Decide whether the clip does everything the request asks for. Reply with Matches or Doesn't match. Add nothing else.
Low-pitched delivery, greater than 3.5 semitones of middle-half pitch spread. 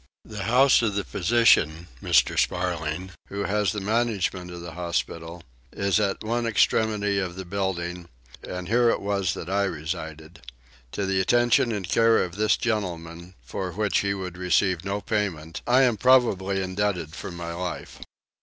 Doesn't match